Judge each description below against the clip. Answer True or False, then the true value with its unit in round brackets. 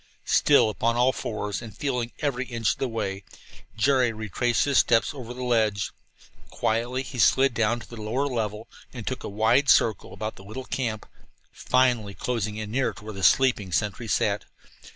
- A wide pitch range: False (2.9 semitones)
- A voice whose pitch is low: True (115 Hz)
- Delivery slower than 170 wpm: False (180 wpm)